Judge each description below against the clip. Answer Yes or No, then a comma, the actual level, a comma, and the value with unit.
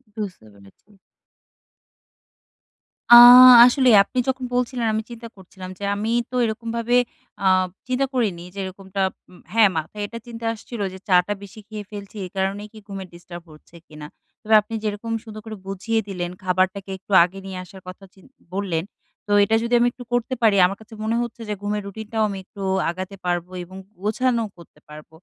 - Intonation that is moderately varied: Yes, average, 3.3 semitones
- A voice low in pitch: No, high, 205 Hz